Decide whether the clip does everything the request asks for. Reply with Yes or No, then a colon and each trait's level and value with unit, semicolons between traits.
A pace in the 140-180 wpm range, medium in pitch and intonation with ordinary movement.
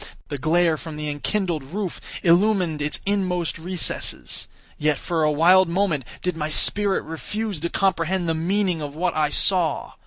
Yes: average, 160 wpm; medium, 170 Hz; average, 3.5 semitones